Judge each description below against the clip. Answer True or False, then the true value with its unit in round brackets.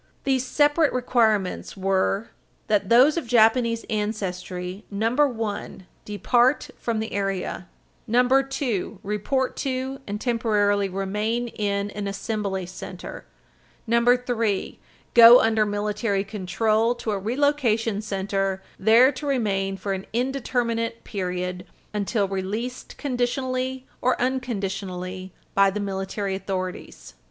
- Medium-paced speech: False (110 wpm)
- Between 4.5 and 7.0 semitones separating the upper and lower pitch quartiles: False (4.0 semitones)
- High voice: True (215 Hz)